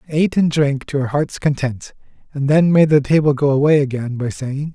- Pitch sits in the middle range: Yes, medium, 145 Hz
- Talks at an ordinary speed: No, fast, 225 wpm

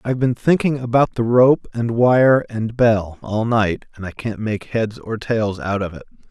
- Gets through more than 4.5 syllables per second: No, 4.4 syllables/s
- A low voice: Yes, low, 115 Hz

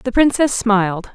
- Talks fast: No, average, 160 wpm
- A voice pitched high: Yes, high, 225 Hz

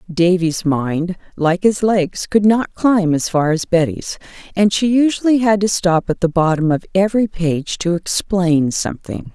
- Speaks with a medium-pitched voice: Yes, medium, 180 Hz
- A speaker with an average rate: Yes, average, 175 wpm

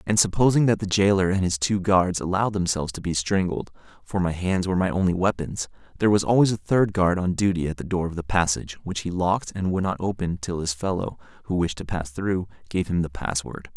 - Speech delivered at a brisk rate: Yes, fast, 225 wpm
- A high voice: No, very low, 90 Hz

